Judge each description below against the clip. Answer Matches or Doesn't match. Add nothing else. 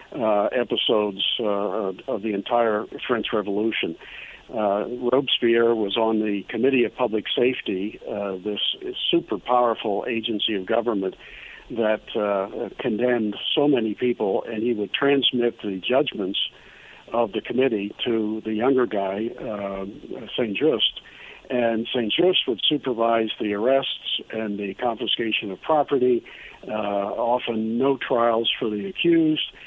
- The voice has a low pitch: Matches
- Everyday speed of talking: Doesn't match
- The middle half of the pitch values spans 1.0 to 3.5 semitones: Matches